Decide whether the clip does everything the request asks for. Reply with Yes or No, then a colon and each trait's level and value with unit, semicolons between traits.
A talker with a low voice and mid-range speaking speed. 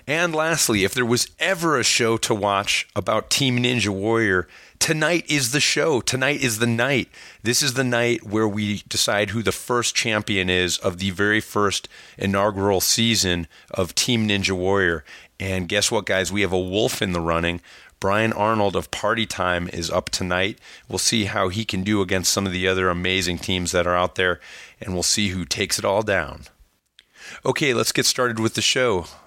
Yes: low, 105 Hz; average, 195 wpm